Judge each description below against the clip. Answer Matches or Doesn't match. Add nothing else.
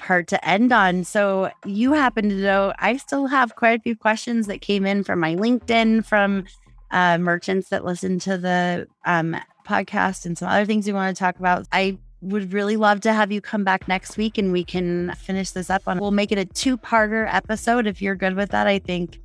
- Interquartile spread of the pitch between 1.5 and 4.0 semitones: Matches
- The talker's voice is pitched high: Matches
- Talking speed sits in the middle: Doesn't match